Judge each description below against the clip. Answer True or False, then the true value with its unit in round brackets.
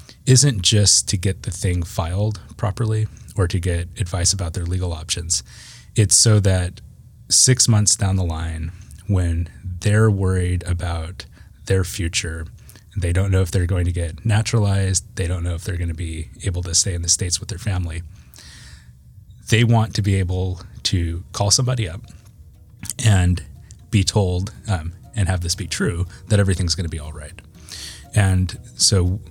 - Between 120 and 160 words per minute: False (170 wpm)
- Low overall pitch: True (95 Hz)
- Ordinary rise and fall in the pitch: True (3.2 semitones)